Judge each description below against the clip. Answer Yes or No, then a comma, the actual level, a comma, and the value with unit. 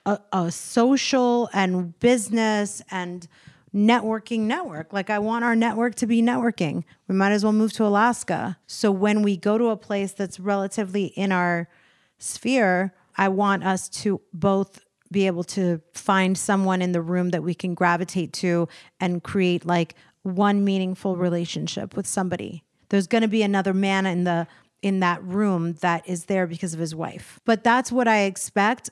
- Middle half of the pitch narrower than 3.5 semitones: Yes, average, 3.0 semitones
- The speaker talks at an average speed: Yes, average, 175 wpm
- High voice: Yes, high, 195 Hz